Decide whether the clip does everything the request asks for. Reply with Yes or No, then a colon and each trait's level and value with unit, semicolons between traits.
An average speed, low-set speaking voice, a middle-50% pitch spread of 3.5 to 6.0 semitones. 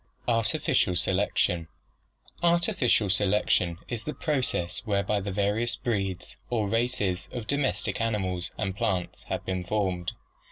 No: slow, 120 wpm; low, 100 Hz; average, 4.0 semitones